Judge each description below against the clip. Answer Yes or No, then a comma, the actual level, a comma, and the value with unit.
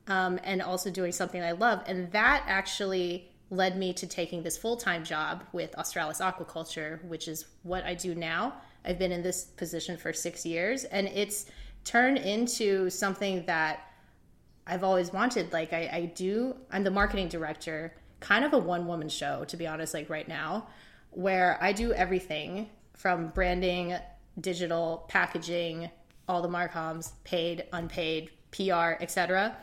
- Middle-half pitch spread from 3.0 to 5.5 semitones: No, narrow, 2.4 semitones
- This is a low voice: No, medium, 180 Hz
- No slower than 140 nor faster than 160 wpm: Yes, average, 155 wpm